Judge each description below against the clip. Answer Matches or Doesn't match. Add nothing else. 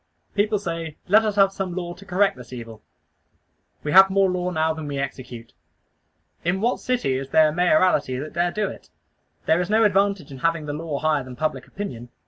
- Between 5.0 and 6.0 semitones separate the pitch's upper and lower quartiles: Matches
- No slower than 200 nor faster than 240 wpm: Matches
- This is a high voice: Doesn't match